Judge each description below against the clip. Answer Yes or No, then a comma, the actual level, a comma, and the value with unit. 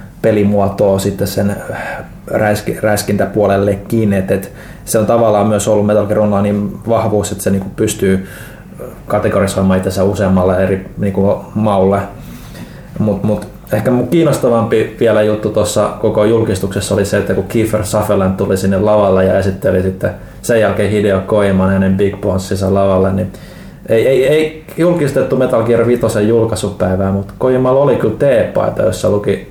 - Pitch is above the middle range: No, low, 105 Hz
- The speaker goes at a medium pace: Yes, average, 140 wpm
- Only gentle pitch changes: Yes, narrow, 2.0 semitones